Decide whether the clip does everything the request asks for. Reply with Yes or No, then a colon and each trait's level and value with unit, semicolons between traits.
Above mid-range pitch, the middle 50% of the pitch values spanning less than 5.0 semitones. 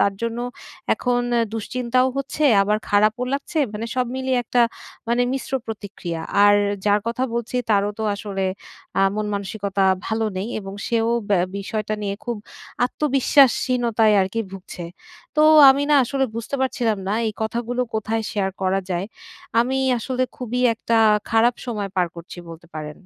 Yes: high, 225 Hz; average, 3.6 semitones